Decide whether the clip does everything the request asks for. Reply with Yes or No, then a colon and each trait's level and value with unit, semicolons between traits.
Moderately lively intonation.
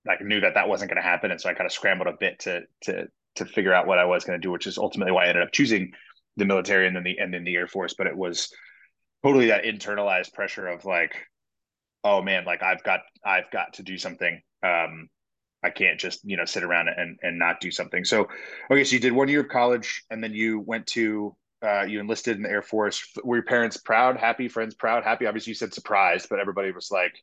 Yes: average, 3.4 semitones